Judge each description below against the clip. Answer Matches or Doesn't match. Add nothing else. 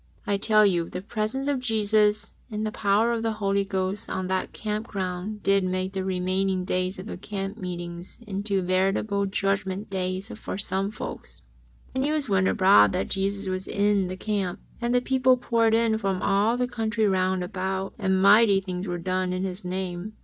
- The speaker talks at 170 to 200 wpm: Matches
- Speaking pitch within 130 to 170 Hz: Doesn't match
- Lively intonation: Doesn't match